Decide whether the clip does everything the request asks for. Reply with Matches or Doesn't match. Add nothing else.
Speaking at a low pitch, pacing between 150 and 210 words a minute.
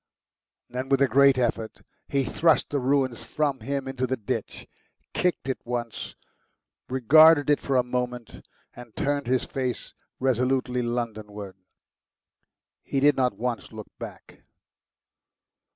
Doesn't match